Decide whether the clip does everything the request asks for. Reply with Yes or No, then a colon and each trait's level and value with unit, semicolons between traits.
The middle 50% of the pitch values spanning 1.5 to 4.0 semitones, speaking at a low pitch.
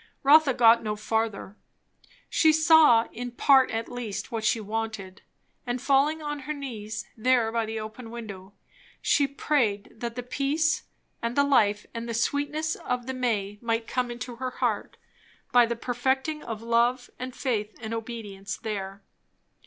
No: average, 3.2 semitones; high, 235 Hz